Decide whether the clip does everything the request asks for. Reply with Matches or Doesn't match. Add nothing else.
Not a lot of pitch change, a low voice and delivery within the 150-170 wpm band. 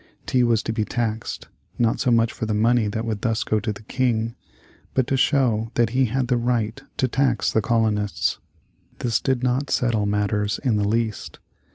Doesn't match